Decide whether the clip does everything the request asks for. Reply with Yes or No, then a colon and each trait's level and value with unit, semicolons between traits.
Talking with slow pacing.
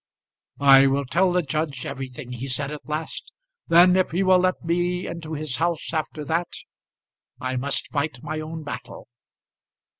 No: average, 160 wpm